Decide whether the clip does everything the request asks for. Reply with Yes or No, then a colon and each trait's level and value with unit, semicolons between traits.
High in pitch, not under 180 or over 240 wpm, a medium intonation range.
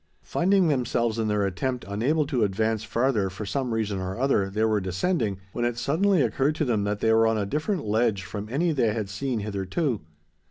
No: low, 115 Hz; fast, 205 wpm; average, 4.9 semitones